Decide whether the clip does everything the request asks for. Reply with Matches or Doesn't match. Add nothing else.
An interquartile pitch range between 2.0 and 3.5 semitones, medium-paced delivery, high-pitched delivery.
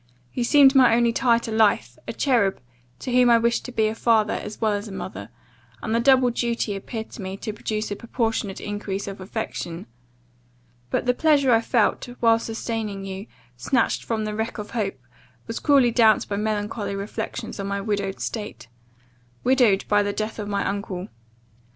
Matches